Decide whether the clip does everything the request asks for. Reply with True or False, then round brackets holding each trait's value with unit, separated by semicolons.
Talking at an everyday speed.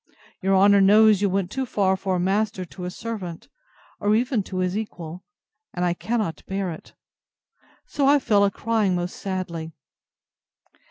True (165 wpm)